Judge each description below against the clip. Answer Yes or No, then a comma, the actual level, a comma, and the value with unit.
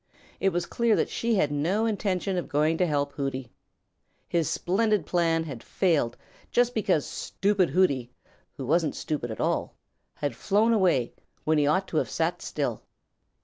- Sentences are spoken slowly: No, average, 165 wpm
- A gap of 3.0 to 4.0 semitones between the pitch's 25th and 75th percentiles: No, average, 5.3 semitones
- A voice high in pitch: No, medium, 170 Hz